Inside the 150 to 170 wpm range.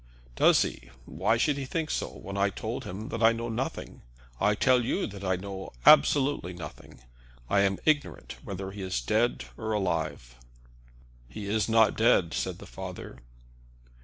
Yes: average, 165 wpm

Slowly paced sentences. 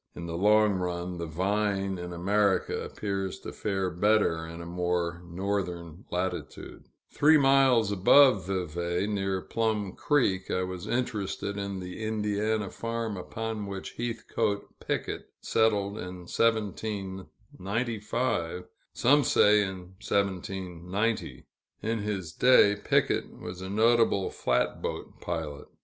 Yes: slow, 120 wpm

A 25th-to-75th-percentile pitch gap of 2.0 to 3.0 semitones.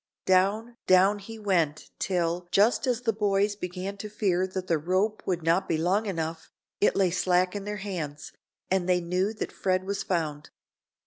Yes: average, 2.7 semitones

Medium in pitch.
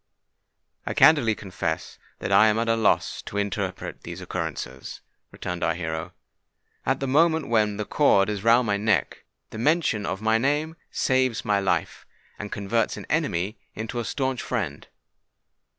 No: low, 110 Hz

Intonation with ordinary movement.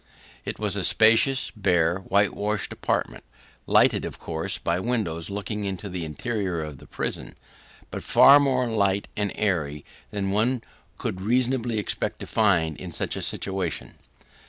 Yes: average, 4.0 semitones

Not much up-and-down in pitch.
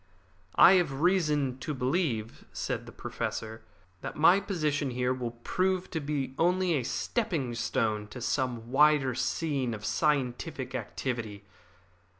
No: average, 4.7 semitones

